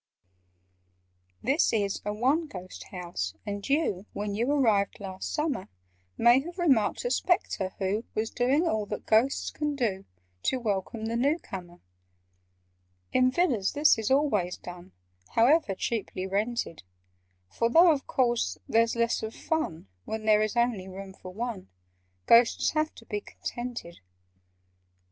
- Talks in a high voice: Yes, high, 225 Hz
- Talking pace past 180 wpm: No, average, 145 wpm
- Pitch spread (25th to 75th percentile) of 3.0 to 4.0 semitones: No, average, 5.2 semitones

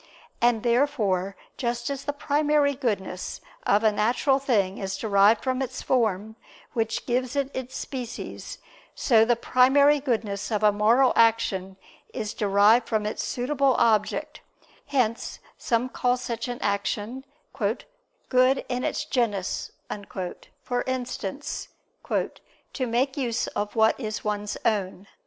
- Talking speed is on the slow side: Yes, slow, 130 wpm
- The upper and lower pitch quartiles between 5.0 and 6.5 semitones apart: No, average, 3.7 semitones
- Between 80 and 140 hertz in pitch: No, high, 235 Hz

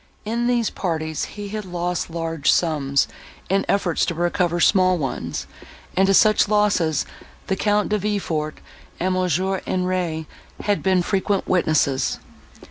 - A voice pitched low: No, medium, 185 Hz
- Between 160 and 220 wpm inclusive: No, slow, 135 wpm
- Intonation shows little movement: No, average, 3.5 semitones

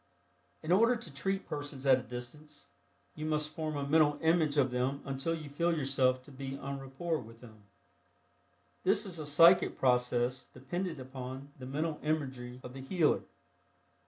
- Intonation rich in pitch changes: No, average, 3.4 semitones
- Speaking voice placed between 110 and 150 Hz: Yes, medium, 140 Hz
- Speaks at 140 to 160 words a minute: No, average, 170 wpm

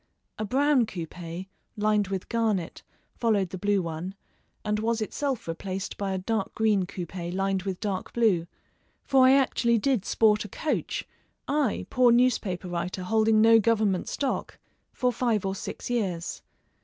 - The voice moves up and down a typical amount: Yes, average, 3.7 semitones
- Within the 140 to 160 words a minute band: Yes, average, 155 wpm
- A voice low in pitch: No, high, 210 Hz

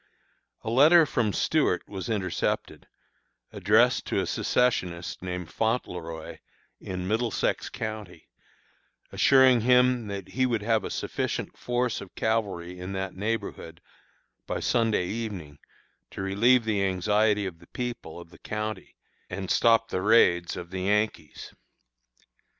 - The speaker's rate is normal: No, slow, 130 wpm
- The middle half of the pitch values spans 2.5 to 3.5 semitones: No, average, 4.1 semitones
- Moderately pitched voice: No, low, 105 Hz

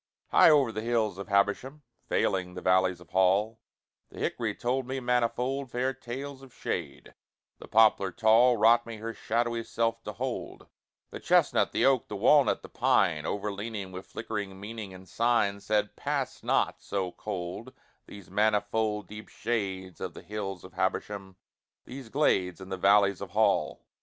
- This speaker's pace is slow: No, average, 160 wpm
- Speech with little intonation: No, average, 3.4 semitones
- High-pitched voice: No, low, 105 Hz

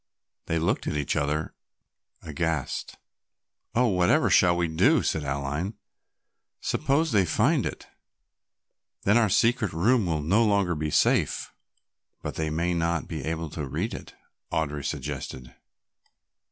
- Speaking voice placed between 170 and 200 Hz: No, very low, 80 Hz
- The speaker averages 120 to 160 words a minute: Yes, average, 140 wpm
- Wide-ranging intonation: No, average, 4.2 semitones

